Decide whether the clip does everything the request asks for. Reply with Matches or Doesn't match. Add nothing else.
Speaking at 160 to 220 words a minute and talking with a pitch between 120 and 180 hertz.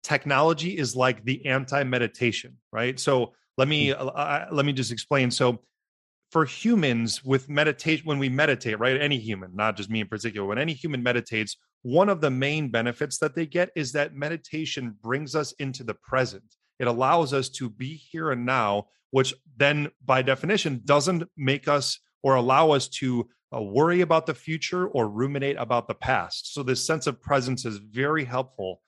Matches